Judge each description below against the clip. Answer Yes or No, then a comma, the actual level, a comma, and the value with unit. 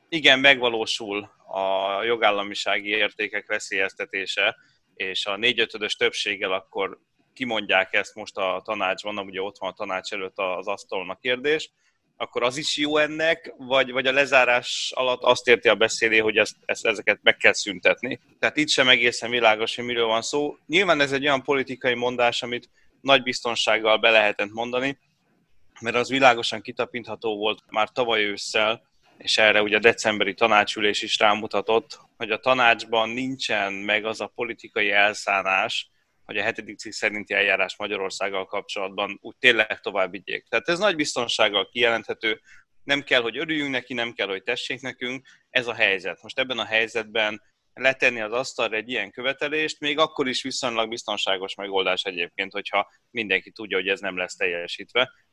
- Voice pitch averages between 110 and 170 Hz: Yes, low, 120 Hz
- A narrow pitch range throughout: No, average, 4.0 semitones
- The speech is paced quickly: Yes, fast, 160 wpm